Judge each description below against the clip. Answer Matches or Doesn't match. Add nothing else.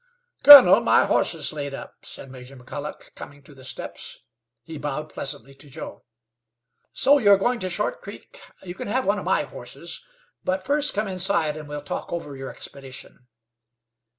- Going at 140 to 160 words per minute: Doesn't match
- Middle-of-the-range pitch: Matches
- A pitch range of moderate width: Doesn't match